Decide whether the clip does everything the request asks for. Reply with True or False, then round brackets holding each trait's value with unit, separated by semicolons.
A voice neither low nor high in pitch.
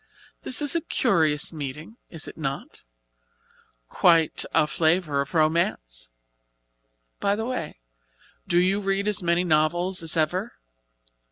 True (170 Hz)